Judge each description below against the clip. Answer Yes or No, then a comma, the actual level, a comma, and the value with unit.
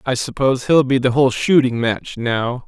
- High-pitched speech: No, low, 125 Hz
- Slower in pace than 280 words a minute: Yes, average, 200 wpm